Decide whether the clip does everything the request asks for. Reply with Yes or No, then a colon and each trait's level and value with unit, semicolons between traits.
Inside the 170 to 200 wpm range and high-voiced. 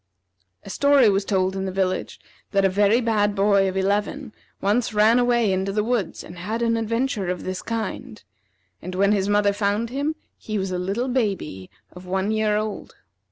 Yes: average, 190 wpm; high, 205 Hz